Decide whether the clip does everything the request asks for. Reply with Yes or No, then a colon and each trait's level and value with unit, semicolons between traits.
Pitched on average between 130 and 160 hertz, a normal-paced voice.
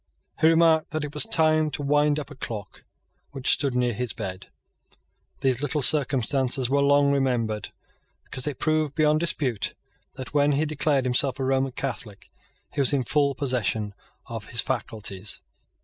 Yes: low, 135 Hz; average, 165 wpm